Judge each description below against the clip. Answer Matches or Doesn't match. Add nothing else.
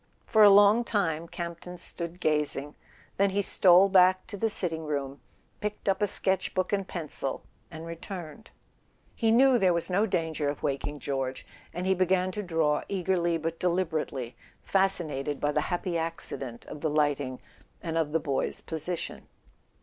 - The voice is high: Doesn't match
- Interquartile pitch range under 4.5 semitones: Matches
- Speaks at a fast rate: Doesn't match